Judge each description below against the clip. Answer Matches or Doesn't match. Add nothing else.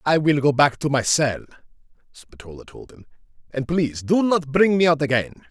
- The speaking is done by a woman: Doesn't match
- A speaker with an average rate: Matches